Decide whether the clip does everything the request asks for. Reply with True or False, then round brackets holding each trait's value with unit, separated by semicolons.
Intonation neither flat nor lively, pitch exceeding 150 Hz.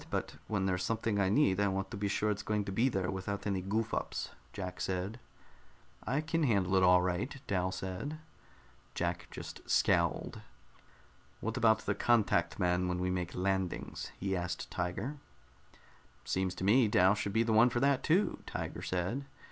False (3.5 semitones; 95 Hz)